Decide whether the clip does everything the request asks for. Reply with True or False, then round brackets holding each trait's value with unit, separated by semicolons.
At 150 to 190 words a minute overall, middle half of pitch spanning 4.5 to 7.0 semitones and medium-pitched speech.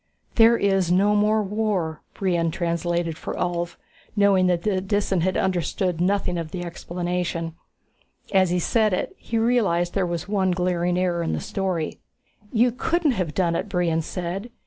False (170 wpm; 2.8 semitones; 180 Hz)